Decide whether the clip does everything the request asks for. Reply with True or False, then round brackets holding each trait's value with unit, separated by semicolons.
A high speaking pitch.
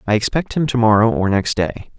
False (115 Hz)